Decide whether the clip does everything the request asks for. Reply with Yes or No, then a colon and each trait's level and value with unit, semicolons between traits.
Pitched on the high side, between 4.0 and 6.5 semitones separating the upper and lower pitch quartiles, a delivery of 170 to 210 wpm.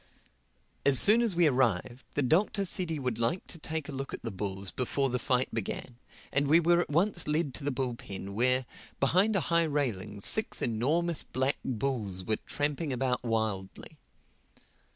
No: low, 135 Hz; wide, 5.6 semitones; average, 180 wpm